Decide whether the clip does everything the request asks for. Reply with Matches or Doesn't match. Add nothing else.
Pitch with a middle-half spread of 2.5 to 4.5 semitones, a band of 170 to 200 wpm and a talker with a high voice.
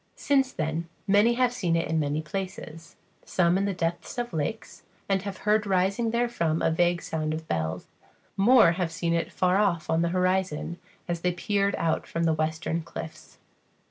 Doesn't match